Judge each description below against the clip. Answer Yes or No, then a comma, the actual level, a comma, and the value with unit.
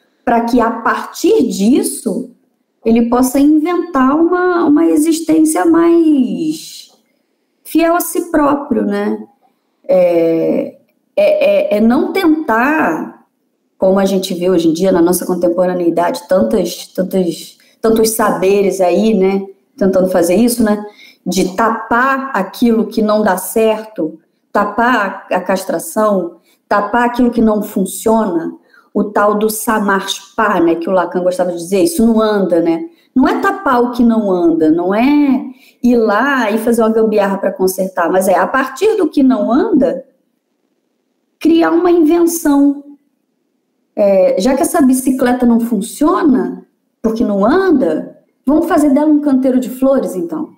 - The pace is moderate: Yes, average, 140 wpm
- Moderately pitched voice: No, high, 240 Hz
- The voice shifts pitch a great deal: Yes, wide, 6.3 semitones